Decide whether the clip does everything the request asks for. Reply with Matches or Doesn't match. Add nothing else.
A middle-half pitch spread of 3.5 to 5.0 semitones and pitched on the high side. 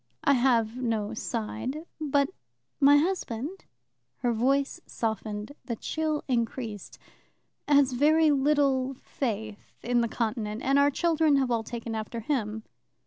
Matches